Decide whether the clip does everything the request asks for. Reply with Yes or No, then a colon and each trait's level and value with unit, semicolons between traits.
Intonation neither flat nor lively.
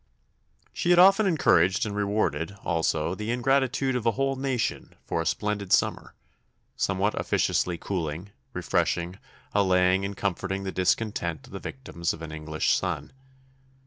No: wide, 5.9 semitones